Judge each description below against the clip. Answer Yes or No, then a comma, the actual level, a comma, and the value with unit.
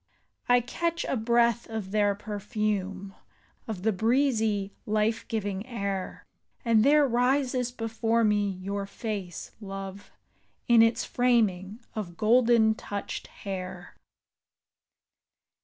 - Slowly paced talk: Yes, slow, 105 wpm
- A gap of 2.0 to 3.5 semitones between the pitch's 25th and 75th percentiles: Yes, average, 3.0 semitones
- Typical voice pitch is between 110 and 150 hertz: No, high, 215 Hz